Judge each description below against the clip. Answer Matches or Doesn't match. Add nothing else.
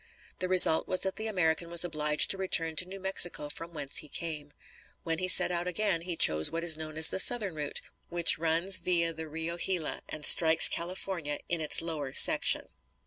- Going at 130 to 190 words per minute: Doesn't match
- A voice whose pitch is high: Doesn't match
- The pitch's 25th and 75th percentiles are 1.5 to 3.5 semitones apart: Matches